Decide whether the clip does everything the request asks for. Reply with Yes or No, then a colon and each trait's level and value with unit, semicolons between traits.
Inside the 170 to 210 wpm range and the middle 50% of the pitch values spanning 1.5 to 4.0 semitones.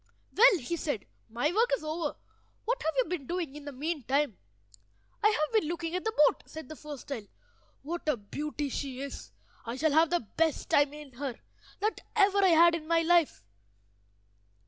Yes: average, 190 wpm; average, 3.4 semitones